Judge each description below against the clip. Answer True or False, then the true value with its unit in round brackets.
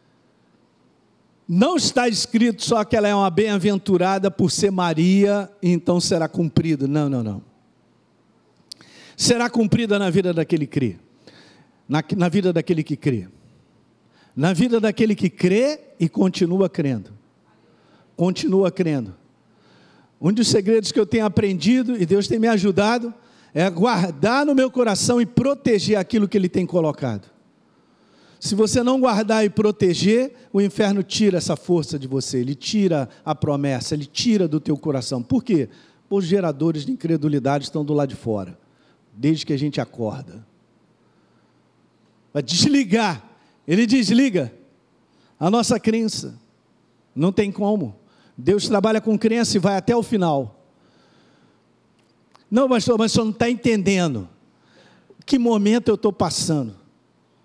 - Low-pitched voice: False (190 Hz)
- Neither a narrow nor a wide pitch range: False (6.3 semitones)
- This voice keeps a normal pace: True (140 wpm)